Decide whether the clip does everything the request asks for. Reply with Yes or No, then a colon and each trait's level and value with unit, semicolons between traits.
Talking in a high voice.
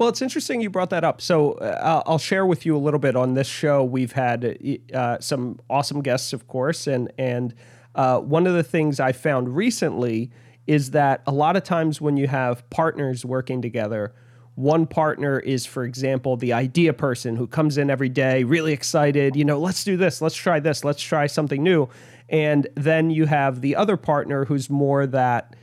No: medium, 140 Hz